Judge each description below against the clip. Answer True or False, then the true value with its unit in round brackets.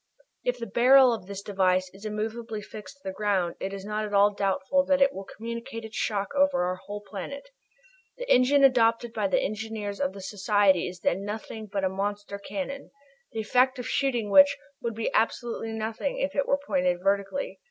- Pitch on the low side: False (215 Hz)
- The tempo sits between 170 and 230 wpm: True (200 wpm)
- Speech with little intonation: False (4.1 semitones)